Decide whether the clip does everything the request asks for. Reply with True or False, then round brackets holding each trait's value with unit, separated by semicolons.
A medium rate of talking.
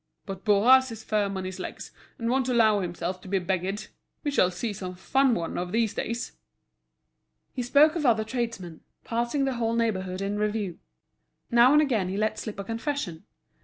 True (185 wpm)